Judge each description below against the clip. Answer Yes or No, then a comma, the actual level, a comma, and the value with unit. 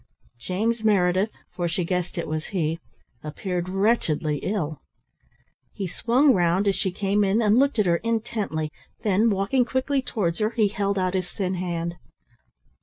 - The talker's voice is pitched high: Yes, high, 195 Hz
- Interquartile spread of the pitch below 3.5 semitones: No, average, 3.8 semitones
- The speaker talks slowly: No, average, 160 wpm